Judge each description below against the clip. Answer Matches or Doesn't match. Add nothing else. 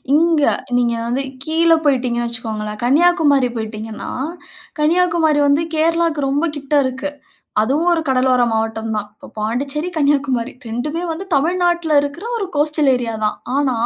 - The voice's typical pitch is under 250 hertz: Doesn't match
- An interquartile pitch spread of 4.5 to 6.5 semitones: Matches